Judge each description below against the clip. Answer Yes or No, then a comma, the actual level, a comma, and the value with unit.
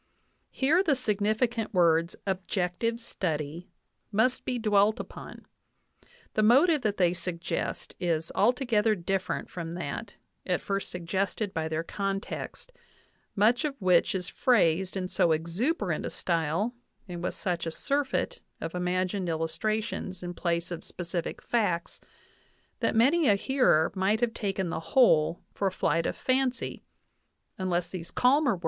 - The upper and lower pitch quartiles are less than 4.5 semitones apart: No, average, 4.9 semitones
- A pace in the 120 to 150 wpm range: Yes, average, 140 wpm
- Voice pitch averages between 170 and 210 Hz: Yes, high, 190 Hz